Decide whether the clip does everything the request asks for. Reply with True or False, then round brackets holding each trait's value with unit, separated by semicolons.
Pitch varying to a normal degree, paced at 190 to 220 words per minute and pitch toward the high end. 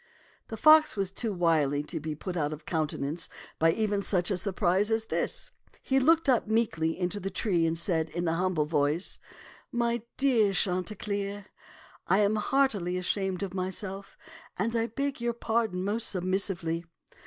False (4.5 semitones; 165 wpm; 195 Hz)